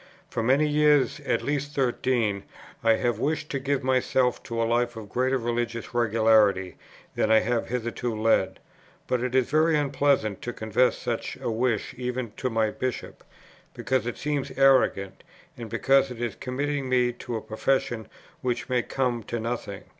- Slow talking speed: No, average, 170 wpm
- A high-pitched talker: No, low, 120 Hz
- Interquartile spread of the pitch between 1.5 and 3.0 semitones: Yes, average, 2.7 semitones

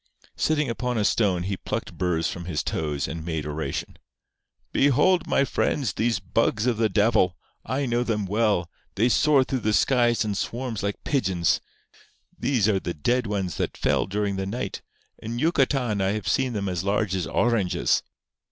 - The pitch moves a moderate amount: Yes, average, 4.6 semitones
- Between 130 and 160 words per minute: No, average, 175 wpm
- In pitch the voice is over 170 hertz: No, low, 105 Hz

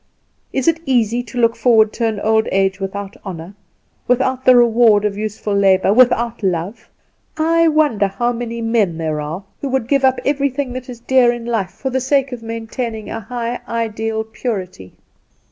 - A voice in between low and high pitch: No, high, 230 Hz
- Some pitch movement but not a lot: Yes, average, 3.5 semitones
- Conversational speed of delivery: Yes, average, 180 wpm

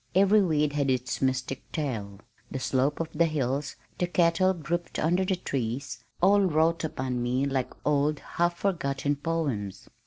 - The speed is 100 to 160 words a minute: Yes, average, 155 wpm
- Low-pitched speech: No, medium, 150 Hz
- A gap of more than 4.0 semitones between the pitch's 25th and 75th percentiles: Yes, average, 4.4 semitones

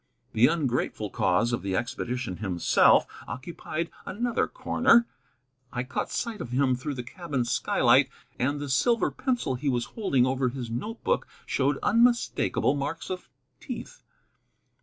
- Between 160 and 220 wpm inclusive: No, average, 140 wpm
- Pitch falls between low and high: No, low, 130 Hz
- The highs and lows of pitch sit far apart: Yes, wide, 6.8 semitones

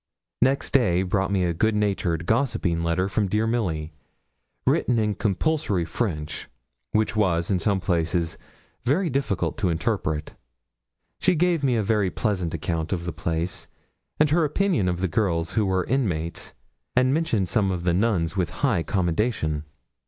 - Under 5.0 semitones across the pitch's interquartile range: No, wide, 5.4 semitones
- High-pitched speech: No, very low, 95 Hz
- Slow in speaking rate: No, average, 155 wpm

